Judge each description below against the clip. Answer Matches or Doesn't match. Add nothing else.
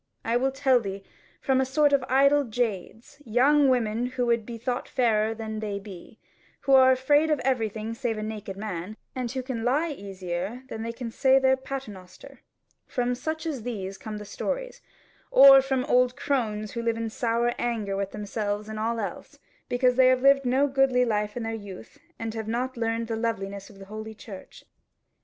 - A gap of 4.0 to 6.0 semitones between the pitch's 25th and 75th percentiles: Doesn't match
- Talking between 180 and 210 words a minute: Matches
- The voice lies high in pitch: Matches